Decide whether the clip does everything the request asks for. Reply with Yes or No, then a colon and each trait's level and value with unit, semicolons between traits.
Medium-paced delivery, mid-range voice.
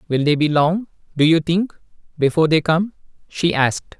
Yes: average, 180 wpm; medium, 160 Hz